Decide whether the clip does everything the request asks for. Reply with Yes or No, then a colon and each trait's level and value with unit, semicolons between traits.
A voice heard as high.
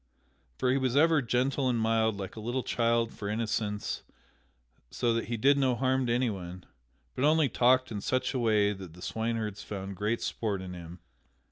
No: low, 115 Hz